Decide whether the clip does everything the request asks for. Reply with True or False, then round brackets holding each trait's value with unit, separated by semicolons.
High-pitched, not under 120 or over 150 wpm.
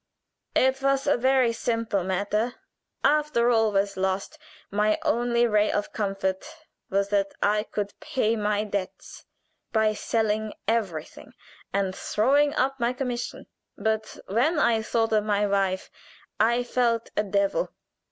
True (220 Hz; 135 wpm)